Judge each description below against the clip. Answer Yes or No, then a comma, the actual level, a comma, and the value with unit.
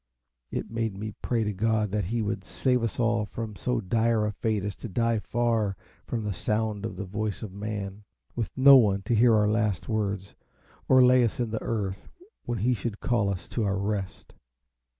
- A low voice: Yes, low, 110 Hz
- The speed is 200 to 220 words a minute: Yes, fast, 205 wpm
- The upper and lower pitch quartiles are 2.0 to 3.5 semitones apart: Yes, narrow, 2.4 semitones